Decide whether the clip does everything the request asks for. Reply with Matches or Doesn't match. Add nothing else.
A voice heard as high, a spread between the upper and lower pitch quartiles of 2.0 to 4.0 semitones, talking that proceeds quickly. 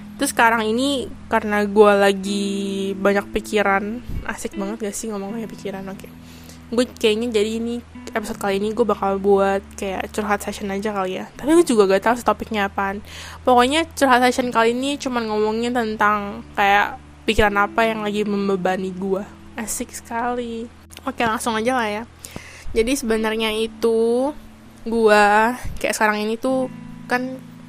Matches